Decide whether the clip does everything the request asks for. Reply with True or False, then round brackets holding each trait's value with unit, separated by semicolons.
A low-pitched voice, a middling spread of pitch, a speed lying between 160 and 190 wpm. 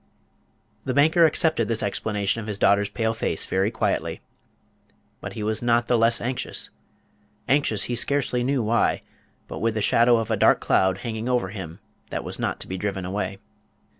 True (115 Hz; 3.2 semitones; 180 wpm)